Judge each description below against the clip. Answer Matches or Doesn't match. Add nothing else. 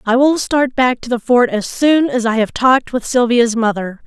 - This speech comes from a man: Doesn't match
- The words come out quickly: Matches